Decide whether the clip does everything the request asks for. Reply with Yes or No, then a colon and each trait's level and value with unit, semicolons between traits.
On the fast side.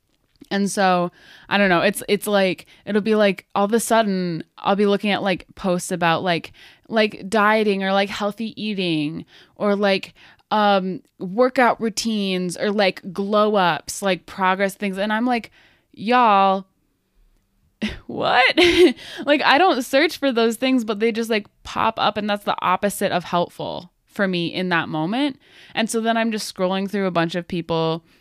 No: average, 170 wpm